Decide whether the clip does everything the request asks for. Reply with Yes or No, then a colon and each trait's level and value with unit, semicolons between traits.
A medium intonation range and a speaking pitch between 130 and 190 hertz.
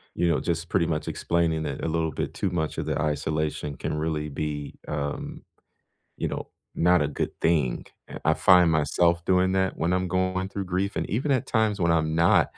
No: average, 3.2 semitones; very low, 85 Hz